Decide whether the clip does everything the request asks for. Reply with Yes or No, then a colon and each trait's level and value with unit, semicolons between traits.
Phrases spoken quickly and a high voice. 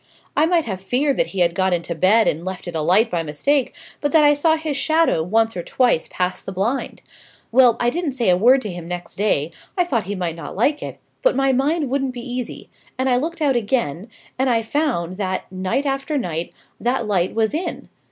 Yes: fast, 220 wpm; high, 230 Hz